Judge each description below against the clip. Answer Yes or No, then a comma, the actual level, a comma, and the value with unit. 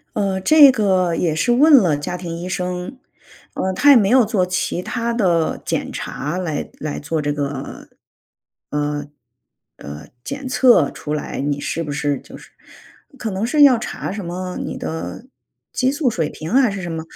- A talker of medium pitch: Yes, medium, 180 Hz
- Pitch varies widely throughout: Yes, wide, 7.1 semitones